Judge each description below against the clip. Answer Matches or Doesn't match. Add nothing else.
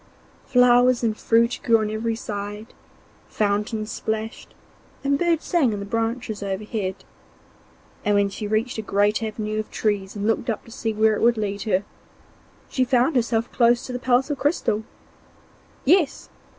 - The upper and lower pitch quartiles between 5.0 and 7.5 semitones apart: Doesn't match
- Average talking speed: Matches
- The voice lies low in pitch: Doesn't match